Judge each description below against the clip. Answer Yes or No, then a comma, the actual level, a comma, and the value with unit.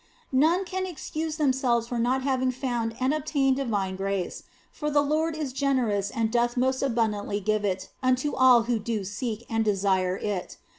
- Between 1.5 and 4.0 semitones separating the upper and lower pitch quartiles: No, average, 4.4 semitones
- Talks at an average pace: Yes, average, 170 wpm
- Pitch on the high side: Yes, high, 245 Hz